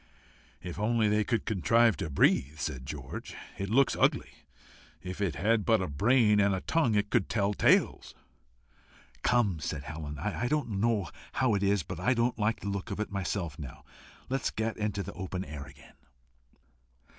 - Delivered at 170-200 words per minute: Yes, average, 180 wpm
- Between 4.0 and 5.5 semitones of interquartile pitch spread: Yes, average, 4.5 semitones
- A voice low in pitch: Yes, low, 100 Hz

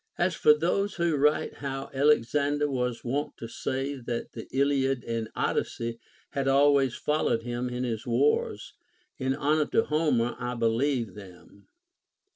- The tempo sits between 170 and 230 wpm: No, average, 145 wpm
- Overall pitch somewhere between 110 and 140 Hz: Yes, low, 135 Hz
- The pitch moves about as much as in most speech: Yes, average, 3.6 semitones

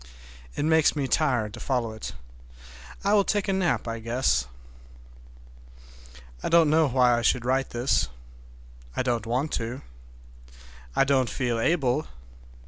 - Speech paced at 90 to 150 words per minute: Yes, average, 140 wpm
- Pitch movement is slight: No, average, 4.6 semitones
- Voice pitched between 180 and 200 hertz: No, low, 130 Hz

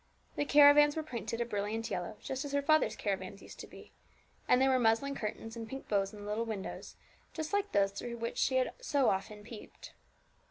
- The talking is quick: Yes, fast, 210 wpm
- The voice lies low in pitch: No, high, 230 Hz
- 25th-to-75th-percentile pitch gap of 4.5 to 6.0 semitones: Yes, average, 5.2 semitones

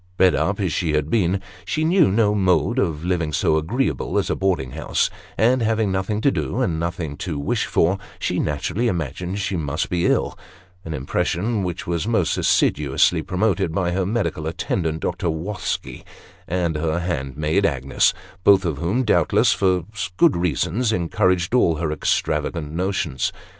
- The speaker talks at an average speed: Yes, average, 165 wpm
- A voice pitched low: Yes, very low, 90 Hz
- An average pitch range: Yes, average, 4.0 semitones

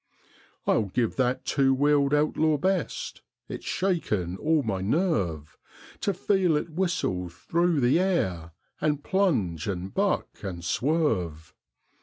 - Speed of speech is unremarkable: No, slow, 125 wpm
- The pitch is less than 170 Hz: Yes, medium, 140 Hz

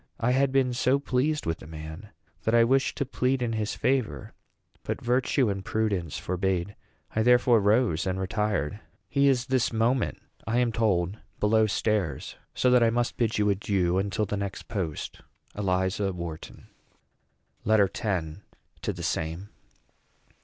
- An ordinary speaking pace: Yes, average, 155 wpm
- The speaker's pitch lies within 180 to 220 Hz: No, low, 105 Hz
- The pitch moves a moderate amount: Yes, average, 4.7 semitones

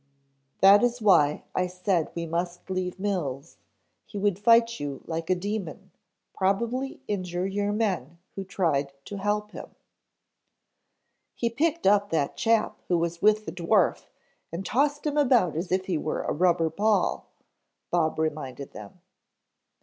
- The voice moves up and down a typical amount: Yes, average, 4.0 semitones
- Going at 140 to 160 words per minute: Yes, average, 150 wpm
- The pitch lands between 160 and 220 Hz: Yes, medium, 185 Hz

